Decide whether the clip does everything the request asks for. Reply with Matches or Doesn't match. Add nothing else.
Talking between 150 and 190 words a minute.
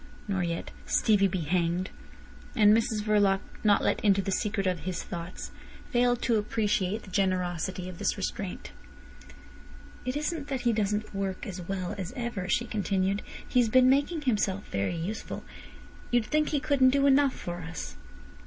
Matches